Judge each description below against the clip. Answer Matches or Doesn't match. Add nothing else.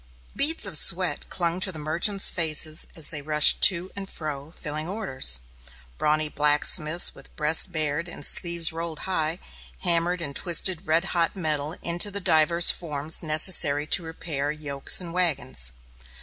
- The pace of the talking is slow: Doesn't match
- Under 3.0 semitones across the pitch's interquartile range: Matches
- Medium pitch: Matches